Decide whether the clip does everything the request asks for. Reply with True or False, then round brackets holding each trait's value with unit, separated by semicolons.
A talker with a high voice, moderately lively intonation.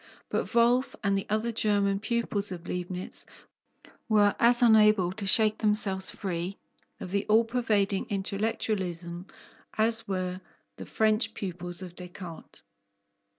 True (200 Hz; 3.0 semitones)